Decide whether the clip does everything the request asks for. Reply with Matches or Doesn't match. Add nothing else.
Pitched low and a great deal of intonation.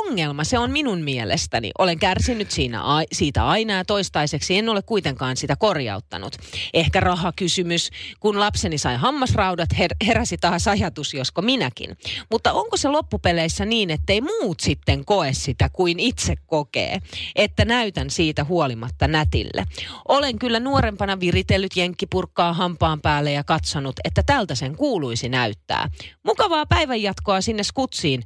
Doesn't match